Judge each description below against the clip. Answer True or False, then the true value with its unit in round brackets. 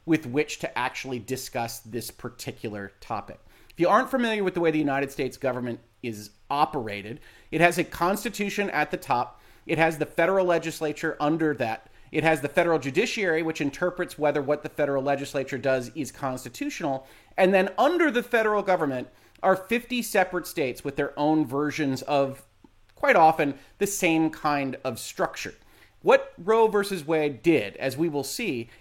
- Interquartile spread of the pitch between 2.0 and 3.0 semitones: False (4.9 semitones)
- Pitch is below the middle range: False (150 Hz)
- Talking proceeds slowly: False (170 wpm)